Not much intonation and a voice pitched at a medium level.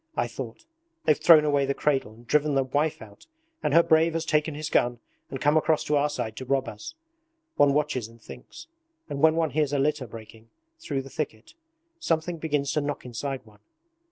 No: average, 3.0 semitones; medium, 145 Hz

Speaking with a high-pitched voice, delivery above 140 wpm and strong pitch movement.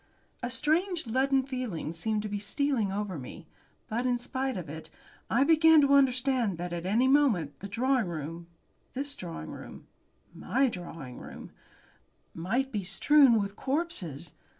Yes: high, 235 Hz; average, 150 wpm; wide, 7.2 semitones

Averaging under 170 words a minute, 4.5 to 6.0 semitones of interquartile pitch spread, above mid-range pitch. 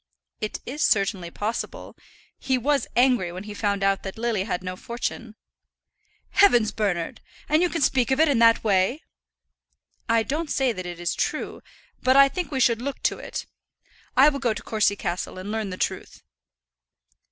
No: average, 175 wpm; average, 5.3 semitones; high, 230 Hz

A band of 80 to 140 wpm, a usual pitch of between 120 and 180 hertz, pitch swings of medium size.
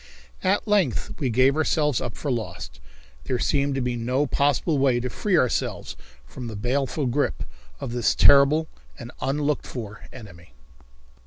No: average, 155 wpm; low, 135 Hz; average, 3.3 semitones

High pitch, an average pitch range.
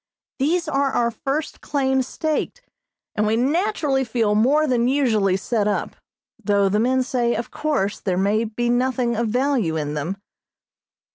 Yes: high, 240 Hz; average, 4.5 semitones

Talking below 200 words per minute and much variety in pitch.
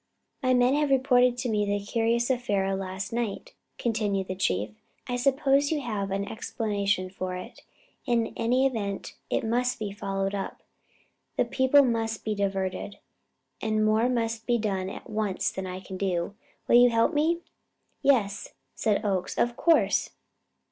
No: average, 160 wpm; average, 3.9 semitones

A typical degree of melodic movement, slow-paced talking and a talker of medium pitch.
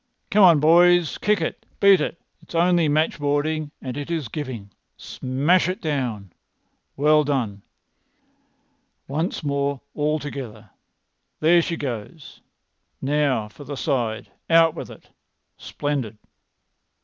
Yes: average, 3.8 semitones; slow, 120 wpm; medium, 145 Hz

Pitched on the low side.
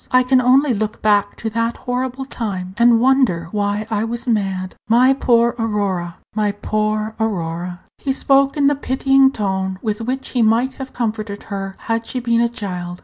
No: high, 225 Hz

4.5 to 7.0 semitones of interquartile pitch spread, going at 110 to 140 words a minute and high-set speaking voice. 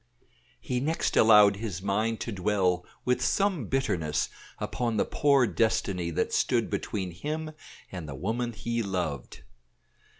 No: average, 5.2 semitones; slow, 135 wpm; low, 105 Hz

